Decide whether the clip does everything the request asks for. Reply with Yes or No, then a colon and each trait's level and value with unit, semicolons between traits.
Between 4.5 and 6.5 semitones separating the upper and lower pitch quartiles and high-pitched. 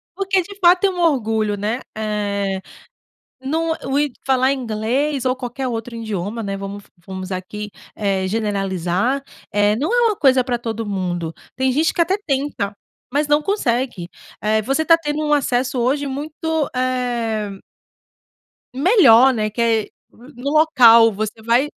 Yes: wide, 5.5 semitones; high, 245 Hz